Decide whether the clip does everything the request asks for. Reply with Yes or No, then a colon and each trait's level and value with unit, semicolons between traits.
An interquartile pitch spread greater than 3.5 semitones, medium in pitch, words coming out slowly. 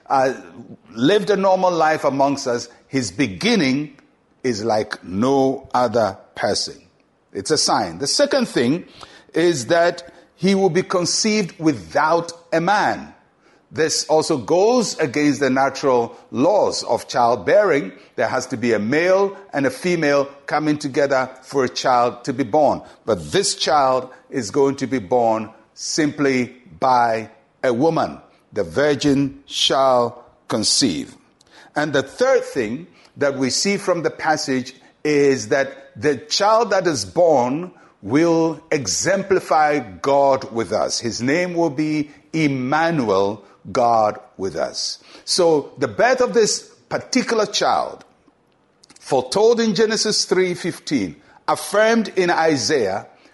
Yes: average, 5.3 semitones; medium, 150 Hz; slow, 130 wpm